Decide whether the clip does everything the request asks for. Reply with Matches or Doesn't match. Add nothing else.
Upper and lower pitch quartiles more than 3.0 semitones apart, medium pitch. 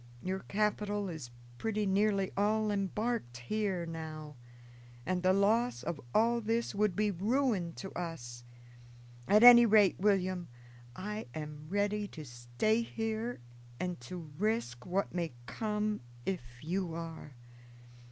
Doesn't match